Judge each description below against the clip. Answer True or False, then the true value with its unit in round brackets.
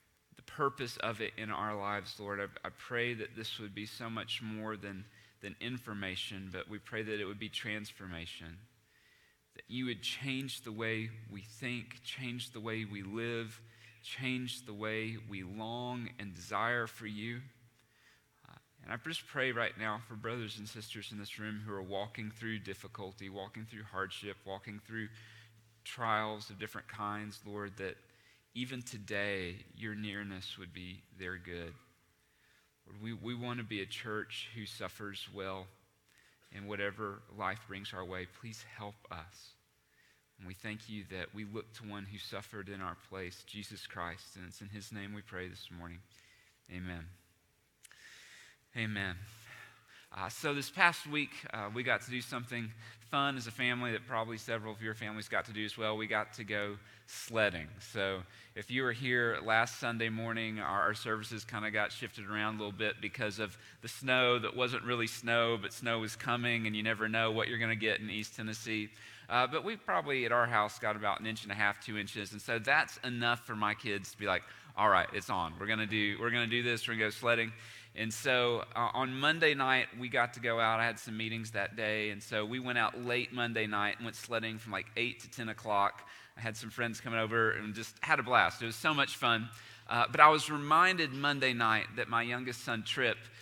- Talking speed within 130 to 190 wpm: False (200 wpm)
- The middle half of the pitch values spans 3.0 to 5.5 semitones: False (2.4 semitones)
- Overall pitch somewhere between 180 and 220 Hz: False (110 Hz)